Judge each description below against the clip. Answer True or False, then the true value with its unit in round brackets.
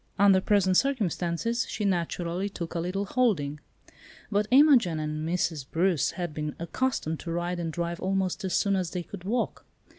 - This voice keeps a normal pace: True (170 wpm)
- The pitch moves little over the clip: False (3.2 semitones)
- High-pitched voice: False (180 Hz)